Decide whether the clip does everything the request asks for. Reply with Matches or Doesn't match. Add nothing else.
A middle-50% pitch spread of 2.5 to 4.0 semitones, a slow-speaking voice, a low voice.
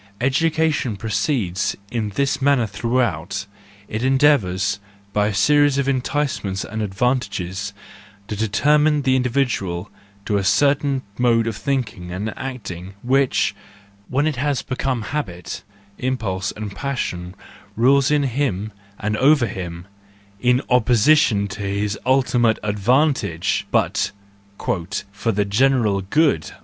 Doesn't match